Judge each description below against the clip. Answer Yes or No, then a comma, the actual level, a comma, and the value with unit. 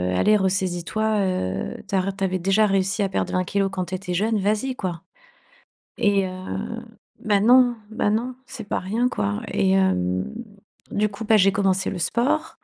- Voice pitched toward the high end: Yes, high, 195 Hz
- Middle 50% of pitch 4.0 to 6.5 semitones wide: No, narrow, 2.6 semitones